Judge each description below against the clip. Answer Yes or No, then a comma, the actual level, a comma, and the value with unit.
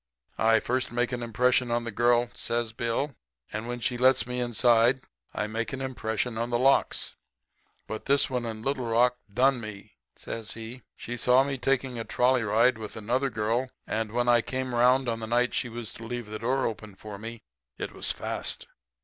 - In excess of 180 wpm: Yes, average, 200 wpm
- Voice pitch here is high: No, low, 120 Hz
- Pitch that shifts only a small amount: Yes, narrow, 2.0 semitones